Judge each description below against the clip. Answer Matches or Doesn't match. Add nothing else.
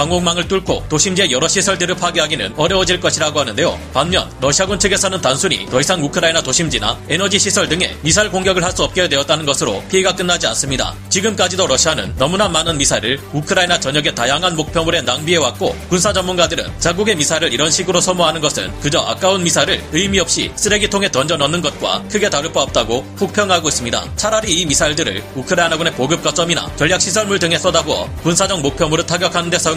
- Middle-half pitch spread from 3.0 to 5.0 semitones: Matches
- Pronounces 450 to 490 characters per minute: Matches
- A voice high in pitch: Doesn't match